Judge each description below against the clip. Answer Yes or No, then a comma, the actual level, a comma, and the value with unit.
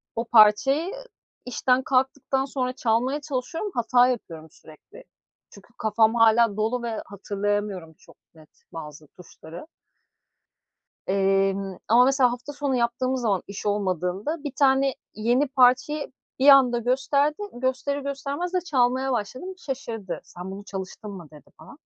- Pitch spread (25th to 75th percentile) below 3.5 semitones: No, average, 5.0 semitones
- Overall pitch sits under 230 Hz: No, high, 245 Hz